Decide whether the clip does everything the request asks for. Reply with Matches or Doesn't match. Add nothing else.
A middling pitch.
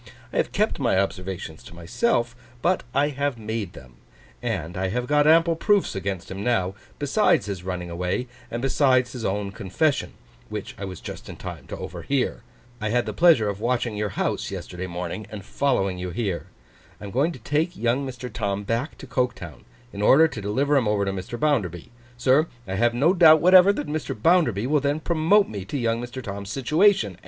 Doesn't match